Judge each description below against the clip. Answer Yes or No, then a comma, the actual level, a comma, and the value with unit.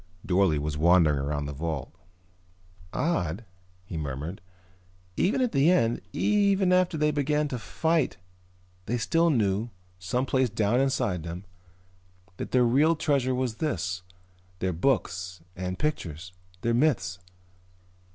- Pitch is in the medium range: No, low, 115 Hz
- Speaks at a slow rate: Yes, slow, 130 wpm